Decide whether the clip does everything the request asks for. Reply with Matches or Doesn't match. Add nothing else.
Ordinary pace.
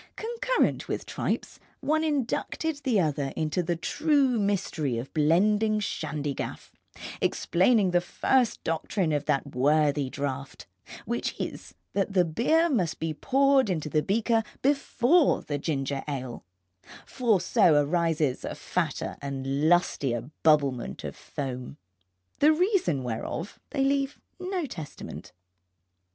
Doesn't match